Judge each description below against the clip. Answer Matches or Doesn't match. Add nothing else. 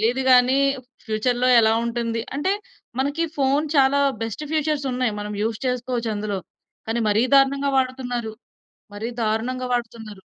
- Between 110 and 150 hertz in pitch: Doesn't match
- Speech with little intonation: Doesn't match